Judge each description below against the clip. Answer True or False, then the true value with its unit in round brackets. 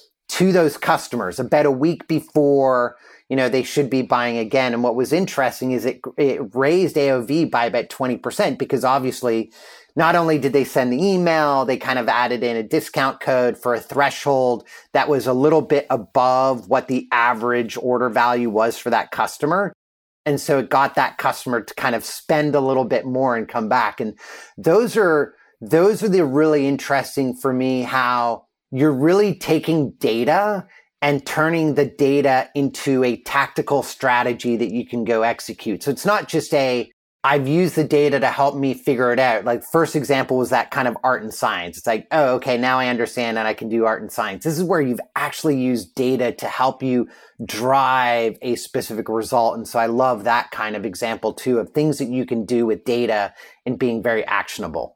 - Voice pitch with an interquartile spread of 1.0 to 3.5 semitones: True (3.2 semitones)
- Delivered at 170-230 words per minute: True (200 wpm)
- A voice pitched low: True (130 Hz)